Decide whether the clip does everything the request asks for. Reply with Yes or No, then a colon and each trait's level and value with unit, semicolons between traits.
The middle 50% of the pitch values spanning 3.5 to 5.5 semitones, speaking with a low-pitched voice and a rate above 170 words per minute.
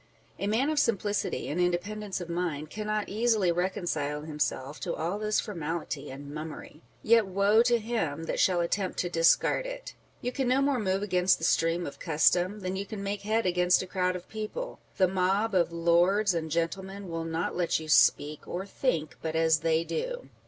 No: average, 4.3 semitones; medium, 185 Hz; average, 190 wpm